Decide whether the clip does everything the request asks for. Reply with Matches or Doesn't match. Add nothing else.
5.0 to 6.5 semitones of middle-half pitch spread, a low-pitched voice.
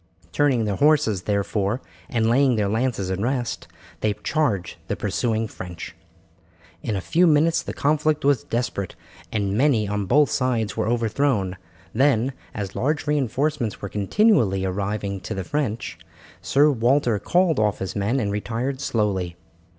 Matches